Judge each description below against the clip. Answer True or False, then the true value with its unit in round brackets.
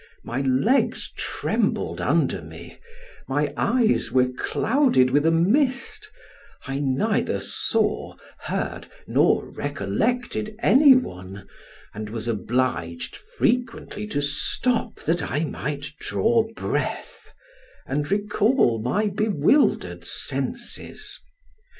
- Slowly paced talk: True (100 wpm)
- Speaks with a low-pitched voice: False (165 Hz)